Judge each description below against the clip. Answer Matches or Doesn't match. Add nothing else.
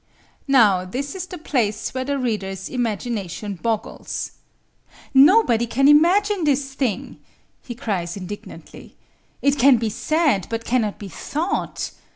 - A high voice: Matches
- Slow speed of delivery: Matches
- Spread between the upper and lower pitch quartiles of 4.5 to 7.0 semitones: Matches